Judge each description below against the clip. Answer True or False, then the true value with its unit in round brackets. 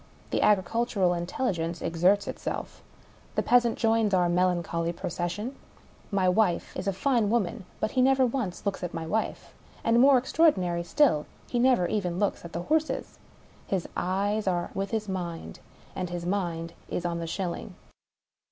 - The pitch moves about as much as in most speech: True (4.6 semitones)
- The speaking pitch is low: False (190 Hz)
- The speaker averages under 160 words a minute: False (170 wpm)